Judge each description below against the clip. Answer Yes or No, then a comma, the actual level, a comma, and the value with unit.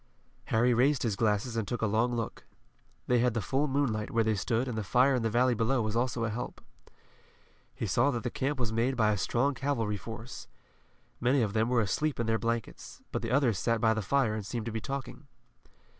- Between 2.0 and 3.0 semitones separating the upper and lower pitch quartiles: Yes, narrow, 2.4 semitones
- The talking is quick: Yes, fast, 225 wpm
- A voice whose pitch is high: No, low, 115 Hz